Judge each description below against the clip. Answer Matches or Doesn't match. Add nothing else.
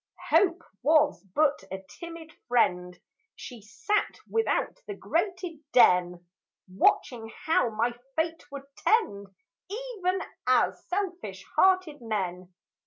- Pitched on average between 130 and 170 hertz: Doesn't match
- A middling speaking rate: Doesn't match